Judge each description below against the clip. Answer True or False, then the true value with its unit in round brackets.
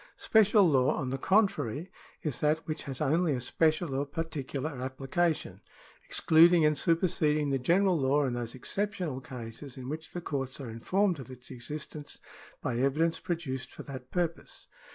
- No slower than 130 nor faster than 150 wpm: False (165 wpm)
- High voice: False (150 Hz)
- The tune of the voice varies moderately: True (4.0 semitones)